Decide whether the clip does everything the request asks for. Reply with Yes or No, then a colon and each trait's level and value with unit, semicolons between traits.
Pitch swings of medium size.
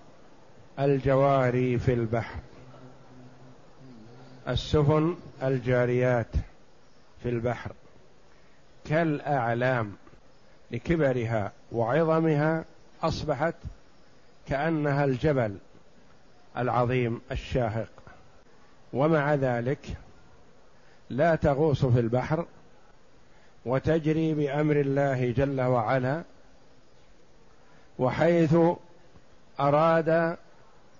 Yes: average, 3.9 semitones